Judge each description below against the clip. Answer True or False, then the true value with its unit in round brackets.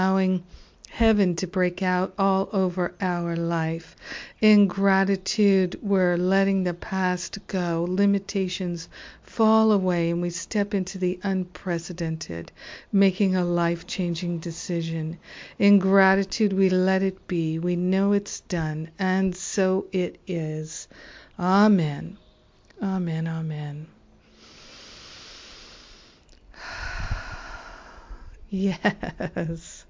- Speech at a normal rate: False (95 wpm)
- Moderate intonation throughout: False (2.2 semitones)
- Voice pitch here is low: False (185 Hz)